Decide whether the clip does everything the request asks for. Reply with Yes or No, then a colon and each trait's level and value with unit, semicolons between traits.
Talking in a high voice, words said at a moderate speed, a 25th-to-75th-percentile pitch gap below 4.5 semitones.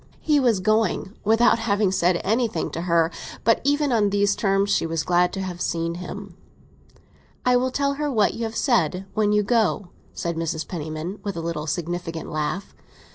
No: high, 195 Hz; average, 175 wpm; average, 4.9 semitones